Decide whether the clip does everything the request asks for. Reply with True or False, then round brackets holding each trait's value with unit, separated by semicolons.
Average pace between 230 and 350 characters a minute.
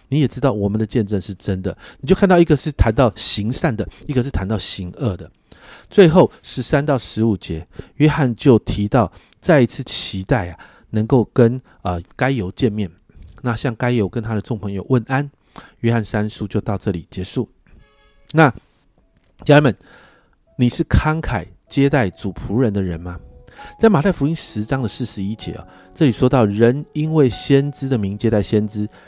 True (260 characters per minute)